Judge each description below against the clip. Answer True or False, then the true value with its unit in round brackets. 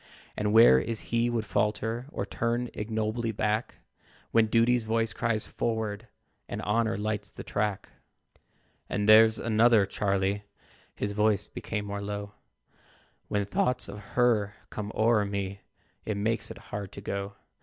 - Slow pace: False (145 wpm)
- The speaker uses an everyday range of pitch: False (2.0 semitones)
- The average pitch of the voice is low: True (105 Hz)